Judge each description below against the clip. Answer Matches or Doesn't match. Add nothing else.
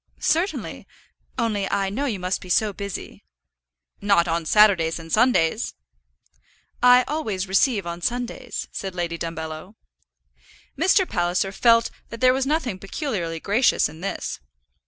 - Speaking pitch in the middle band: Doesn't match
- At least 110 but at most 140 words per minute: Matches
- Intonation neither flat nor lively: Doesn't match